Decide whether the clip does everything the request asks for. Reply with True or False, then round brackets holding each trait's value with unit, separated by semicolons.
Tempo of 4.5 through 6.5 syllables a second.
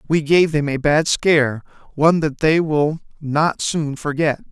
False (4.3 syllables/s)